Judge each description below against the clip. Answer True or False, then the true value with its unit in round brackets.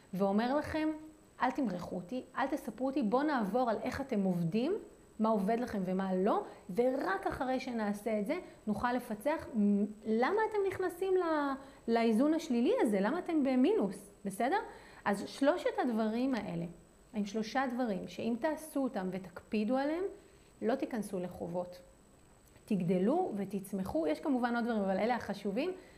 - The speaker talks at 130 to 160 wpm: True (140 wpm)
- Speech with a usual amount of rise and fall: False (6.4 semitones)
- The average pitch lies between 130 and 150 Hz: False (240 Hz)